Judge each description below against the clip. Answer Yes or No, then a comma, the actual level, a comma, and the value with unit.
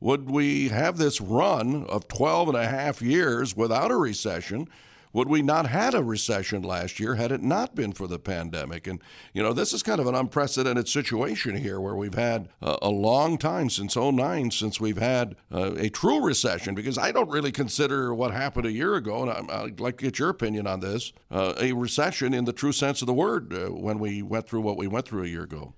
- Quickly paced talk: Yes, fast, 225 wpm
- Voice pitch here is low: Yes, low, 120 Hz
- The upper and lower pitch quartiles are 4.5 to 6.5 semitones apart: Yes, average, 4.9 semitones